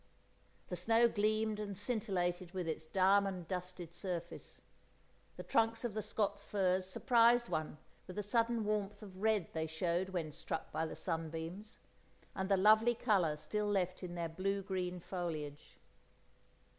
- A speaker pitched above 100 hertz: Yes, high, 190 Hz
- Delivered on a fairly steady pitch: No, average, 3.4 semitones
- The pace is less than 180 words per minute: Yes, average, 150 wpm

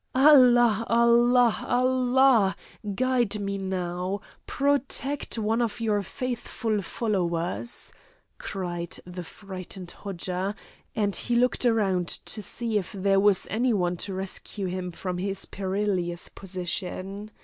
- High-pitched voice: Yes, high, 200 Hz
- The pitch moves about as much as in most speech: Yes, average, 4.3 semitones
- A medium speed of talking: No, slow, 115 wpm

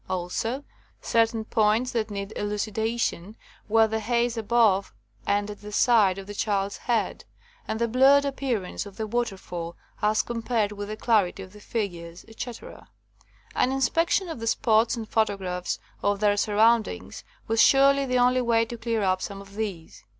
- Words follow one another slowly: No, average, 165 wpm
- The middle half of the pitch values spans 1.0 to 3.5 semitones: Yes, average, 2.8 semitones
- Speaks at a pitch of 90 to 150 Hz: No, high, 220 Hz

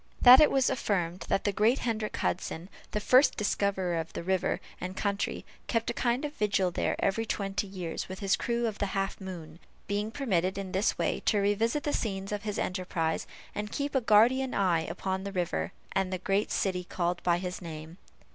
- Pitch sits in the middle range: No, high, 195 Hz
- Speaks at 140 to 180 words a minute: No, average, 200 wpm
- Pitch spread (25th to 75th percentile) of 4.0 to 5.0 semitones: No, average, 3.1 semitones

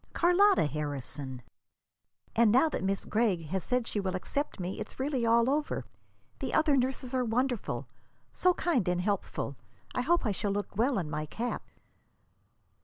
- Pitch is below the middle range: No, high, 230 Hz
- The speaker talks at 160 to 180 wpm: Yes, average, 170 wpm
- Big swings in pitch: Yes, wide, 6.4 semitones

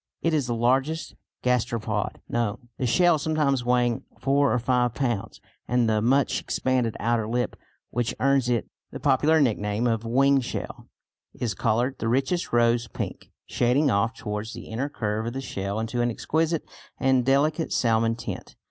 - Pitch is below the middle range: Yes, low, 120 Hz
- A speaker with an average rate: Yes, average, 165 wpm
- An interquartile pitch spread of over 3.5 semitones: No, average, 3.1 semitones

